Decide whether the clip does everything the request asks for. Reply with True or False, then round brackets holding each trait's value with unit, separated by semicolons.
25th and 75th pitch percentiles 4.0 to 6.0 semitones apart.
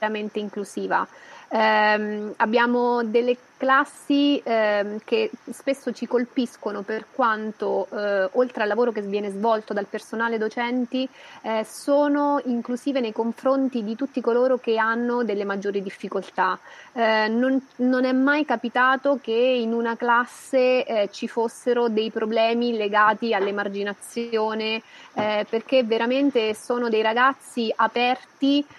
False (2.7 semitones)